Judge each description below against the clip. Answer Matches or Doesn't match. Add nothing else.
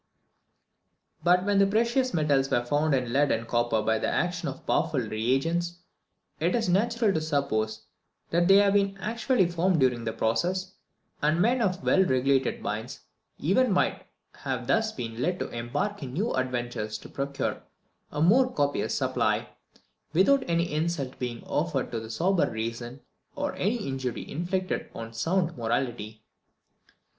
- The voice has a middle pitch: Matches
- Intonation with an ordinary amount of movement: Doesn't match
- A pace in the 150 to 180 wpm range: Matches